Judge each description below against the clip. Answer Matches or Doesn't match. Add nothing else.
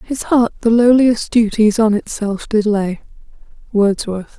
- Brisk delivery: Doesn't match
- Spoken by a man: Doesn't match